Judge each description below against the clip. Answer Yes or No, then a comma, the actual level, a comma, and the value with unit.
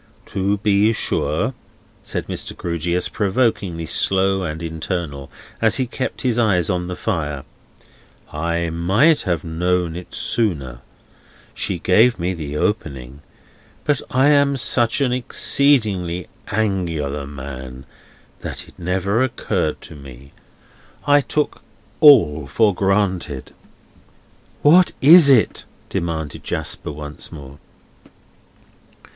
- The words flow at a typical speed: No, slow, 115 wpm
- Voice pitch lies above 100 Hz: No, very low, 90 Hz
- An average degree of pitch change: No, wide, 6.3 semitones